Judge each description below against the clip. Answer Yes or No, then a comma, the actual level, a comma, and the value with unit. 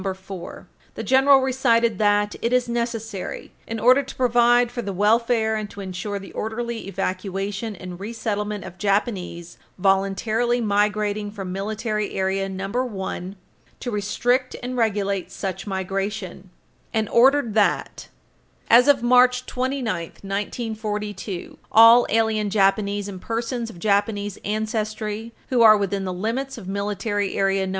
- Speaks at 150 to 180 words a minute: No, average, 140 wpm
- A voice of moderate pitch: No, high, 210 Hz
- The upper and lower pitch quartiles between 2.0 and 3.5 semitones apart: Yes, average, 3.0 semitones